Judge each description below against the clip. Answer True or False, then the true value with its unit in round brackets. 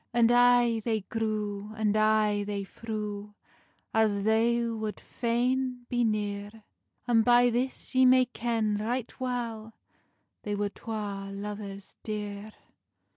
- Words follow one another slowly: True (125 wpm)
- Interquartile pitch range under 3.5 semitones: True (2.5 semitones)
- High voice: True (220 Hz)